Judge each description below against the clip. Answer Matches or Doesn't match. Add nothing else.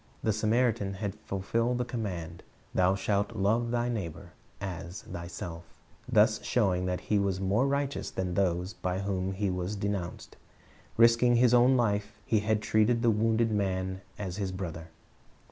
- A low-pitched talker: Matches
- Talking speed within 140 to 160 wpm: Matches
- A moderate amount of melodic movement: Matches